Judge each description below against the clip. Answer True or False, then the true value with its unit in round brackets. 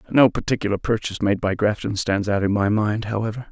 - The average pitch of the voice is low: True (105 Hz)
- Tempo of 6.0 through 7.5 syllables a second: True (6.1 syllables/s)